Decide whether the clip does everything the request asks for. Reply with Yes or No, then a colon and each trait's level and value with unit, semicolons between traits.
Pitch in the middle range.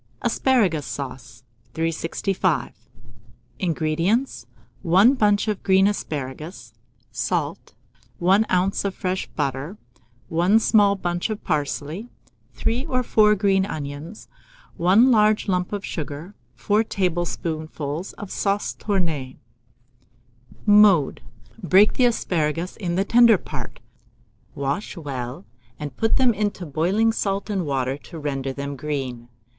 Yes: medium, 180 Hz